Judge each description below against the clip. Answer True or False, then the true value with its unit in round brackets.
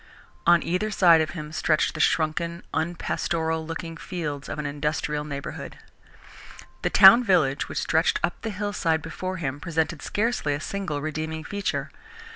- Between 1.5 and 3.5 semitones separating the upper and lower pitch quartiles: True (3.0 semitones)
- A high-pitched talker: False (160 Hz)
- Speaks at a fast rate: False (150 wpm)